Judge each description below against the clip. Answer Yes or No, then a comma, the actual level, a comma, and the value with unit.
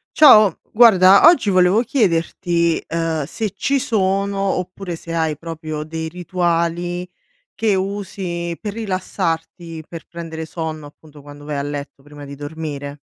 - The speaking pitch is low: No, medium, 170 Hz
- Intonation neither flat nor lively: Yes, average, 3.5 semitones